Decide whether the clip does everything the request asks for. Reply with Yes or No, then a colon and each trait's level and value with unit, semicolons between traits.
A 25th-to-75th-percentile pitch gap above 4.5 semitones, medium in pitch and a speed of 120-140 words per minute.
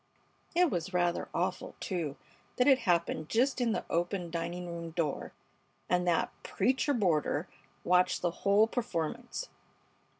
Yes: average, 5.3 semitones; medium, 180 Hz; slow, 135 wpm